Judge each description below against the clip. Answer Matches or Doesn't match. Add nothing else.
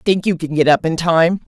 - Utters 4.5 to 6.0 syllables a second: Matches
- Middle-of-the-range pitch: Matches